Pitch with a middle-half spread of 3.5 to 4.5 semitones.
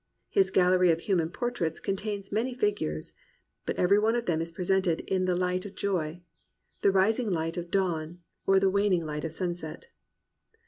No: average, 3.1 semitones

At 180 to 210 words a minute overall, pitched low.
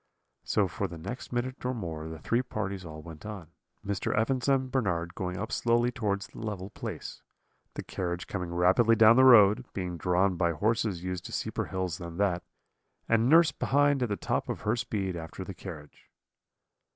Yes: average, 190 wpm; low, 100 Hz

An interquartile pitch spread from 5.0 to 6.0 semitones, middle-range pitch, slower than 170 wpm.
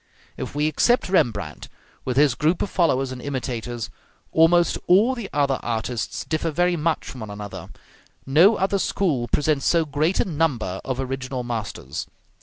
Yes: wide, 5.5 semitones; medium, 145 Hz; average, 160 wpm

